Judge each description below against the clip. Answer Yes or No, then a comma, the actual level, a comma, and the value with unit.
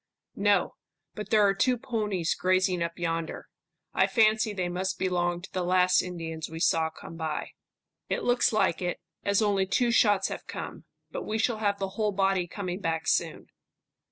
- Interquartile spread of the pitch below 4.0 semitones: Yes, average, 3.1 semitones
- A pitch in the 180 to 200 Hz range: Yes, high, 190 Hz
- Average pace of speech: Yes, average, 180 wpm